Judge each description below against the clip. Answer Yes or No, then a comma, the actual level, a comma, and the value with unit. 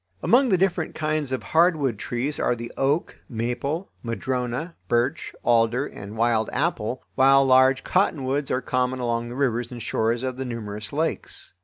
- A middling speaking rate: Yes, average, 160 wpm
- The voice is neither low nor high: No, low, 130 Hz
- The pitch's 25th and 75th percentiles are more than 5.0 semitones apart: No, average, 3.6 semitones